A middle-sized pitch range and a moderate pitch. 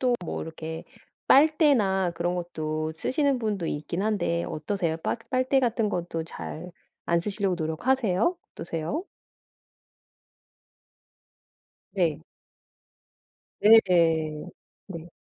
No: wide, 5.9 semitones; medium, 180 Hz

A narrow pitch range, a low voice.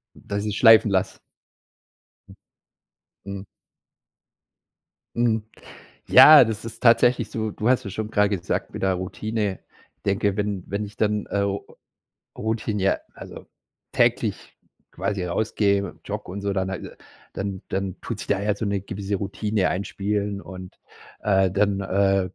Yes: narrow, 1.8 semitones; low, 100 Hz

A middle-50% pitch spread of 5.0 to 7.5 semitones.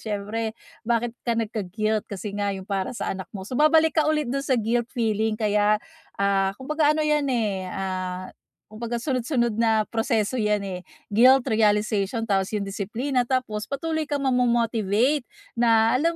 No: average, 3.7 semitones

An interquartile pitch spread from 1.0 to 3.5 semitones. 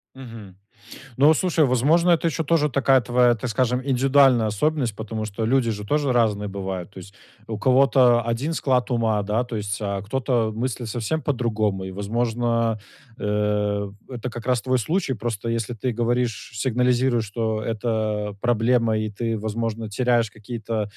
Yes: average, 3.0 semitones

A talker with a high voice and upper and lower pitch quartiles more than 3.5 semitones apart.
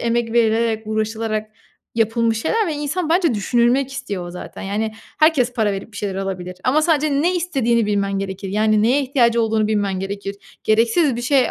Yes: high, 225 Hz; average, 4.4 semitones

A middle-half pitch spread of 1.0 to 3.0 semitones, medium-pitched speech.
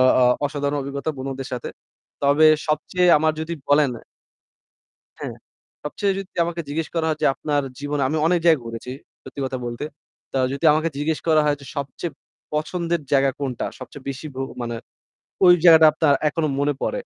Yes: average, 2.7 semitones; medium, 145 Hz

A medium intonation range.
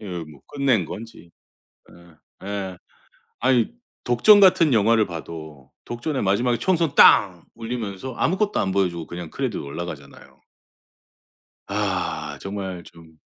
No: wide, 6.2 semitones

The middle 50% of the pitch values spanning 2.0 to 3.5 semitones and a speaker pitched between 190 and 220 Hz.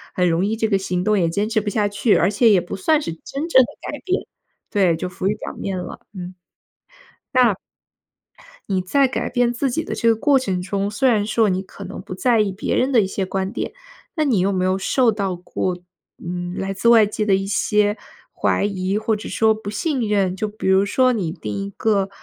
Yes: average, 3.2 semitones; high, 205 Hz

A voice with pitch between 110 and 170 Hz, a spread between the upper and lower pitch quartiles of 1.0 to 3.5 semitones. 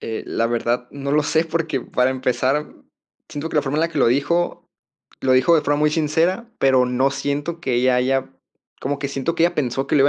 Yes: medium, 140 Hz; average, 3.2 semitones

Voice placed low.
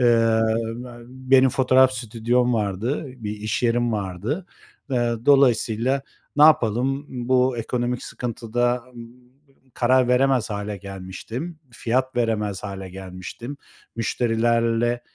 Yes: low, 120 Hz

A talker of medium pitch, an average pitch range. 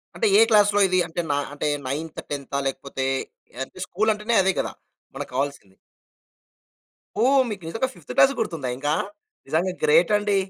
No: medium, 180 Hz; wide, 7.0 semitones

